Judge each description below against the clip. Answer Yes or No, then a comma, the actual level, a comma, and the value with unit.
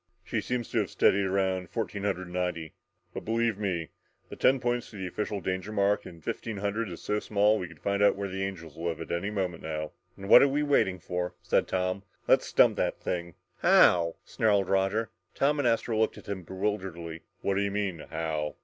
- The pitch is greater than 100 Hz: No, very low, 95 Hz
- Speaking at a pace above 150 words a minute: Yes, fast, 205 wpm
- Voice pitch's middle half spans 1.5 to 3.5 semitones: Yes, average, 3.0 semitones